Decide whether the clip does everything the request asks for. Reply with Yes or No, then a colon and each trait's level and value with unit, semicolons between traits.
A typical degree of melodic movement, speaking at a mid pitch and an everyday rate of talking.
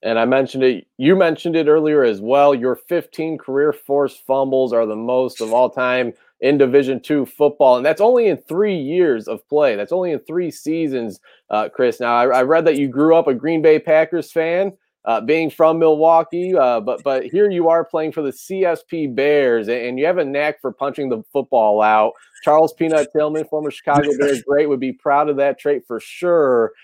No: average, 3.8 semitones; medium, 145 Hz; fast, 210 wpm